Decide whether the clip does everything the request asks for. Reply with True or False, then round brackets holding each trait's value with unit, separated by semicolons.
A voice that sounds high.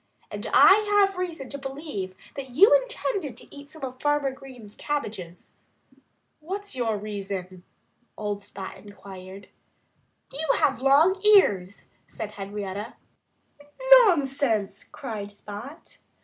True (260 Hz)